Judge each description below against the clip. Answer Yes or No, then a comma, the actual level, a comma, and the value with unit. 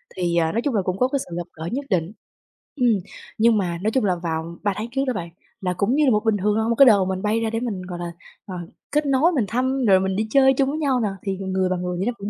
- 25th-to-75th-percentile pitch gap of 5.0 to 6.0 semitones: Yes, average, 5.3 semitones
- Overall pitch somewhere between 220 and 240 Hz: No, high, 210 Hz